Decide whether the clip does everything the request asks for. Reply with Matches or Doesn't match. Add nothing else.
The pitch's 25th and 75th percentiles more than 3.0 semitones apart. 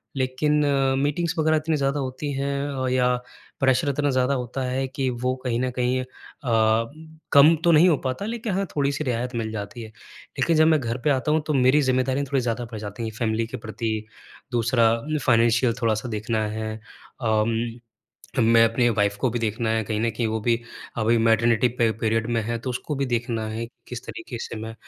Matches